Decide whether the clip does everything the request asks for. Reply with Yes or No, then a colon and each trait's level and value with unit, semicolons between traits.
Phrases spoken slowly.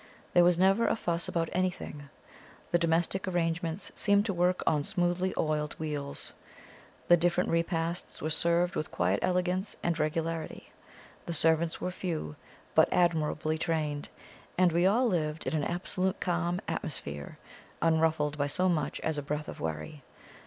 No: average, 150 wpm